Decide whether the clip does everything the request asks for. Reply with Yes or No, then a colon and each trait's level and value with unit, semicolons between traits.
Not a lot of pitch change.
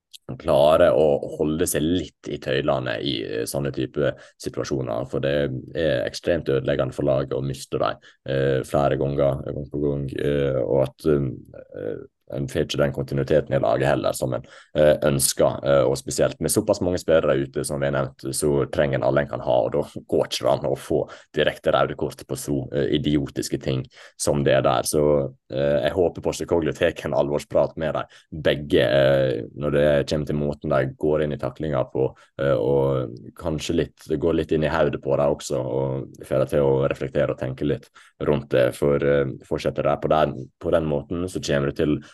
Yes: narrow, 1.6 semitones